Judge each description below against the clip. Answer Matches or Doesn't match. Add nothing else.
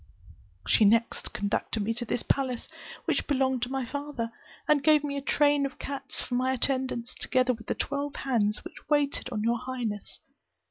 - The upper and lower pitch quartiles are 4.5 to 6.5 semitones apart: Doesn't match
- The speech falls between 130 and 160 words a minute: Doesn't match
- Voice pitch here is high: Matches